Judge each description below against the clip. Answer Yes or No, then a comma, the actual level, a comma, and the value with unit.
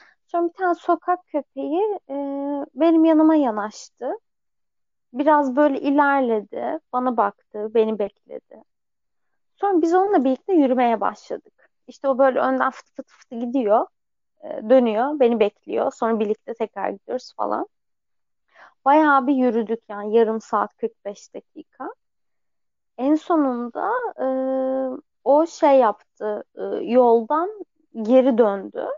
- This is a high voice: Yes, very high, 270 Hz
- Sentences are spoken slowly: No, average, 120 wpm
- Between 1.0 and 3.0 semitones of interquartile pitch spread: No, average, 5.1 semitones